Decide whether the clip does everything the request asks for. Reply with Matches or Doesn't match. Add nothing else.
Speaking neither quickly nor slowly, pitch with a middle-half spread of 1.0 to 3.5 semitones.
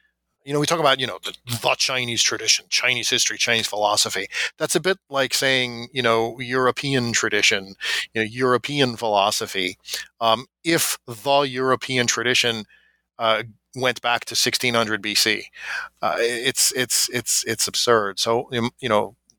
Matches